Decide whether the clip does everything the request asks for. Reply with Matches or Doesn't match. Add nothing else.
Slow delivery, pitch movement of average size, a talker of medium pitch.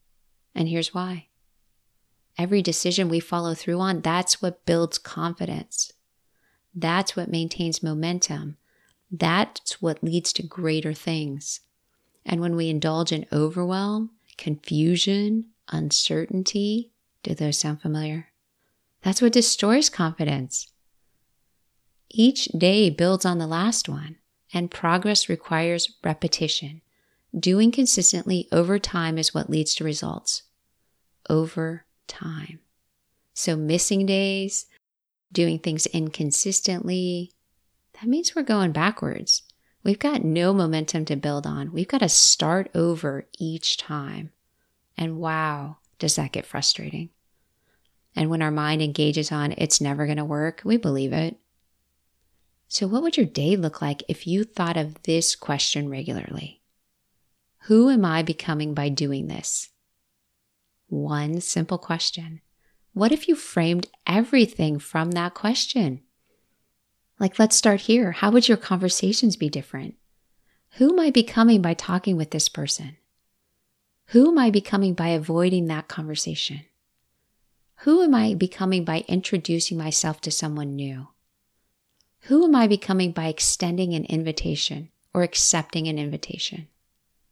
Matches